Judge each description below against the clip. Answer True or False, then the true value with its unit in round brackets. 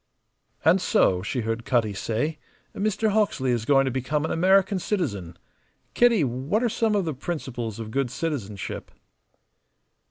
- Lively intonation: True (8.4 semitones)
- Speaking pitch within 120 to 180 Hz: True (140 Hz)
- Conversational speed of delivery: True (150 wpm)